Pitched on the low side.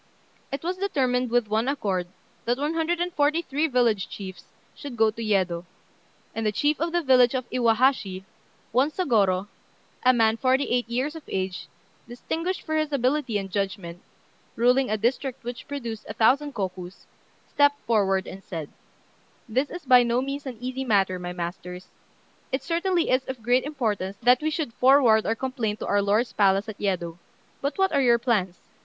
No: high, 240 Hz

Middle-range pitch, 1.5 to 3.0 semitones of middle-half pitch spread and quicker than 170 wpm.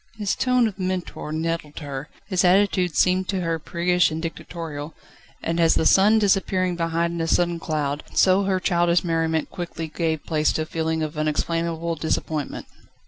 No: medium, 170 Hz; narrow, 2.4 semitones; average, 165 wpm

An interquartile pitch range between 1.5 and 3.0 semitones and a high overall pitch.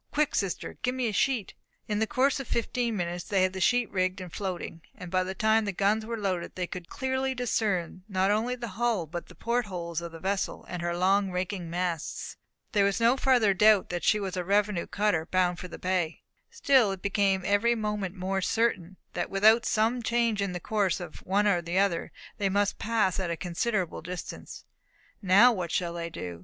No: average, 3.5 semitones; high, 195 Hz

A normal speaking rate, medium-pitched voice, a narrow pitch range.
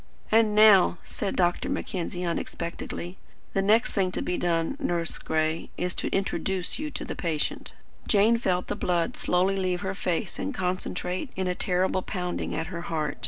Yes: average, 170 wpm; medium, 180 Hz; narrow, 2.1 semitones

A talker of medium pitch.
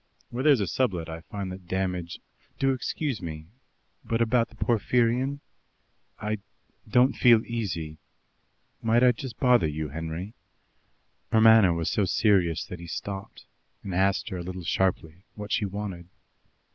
No: low, 100 Hz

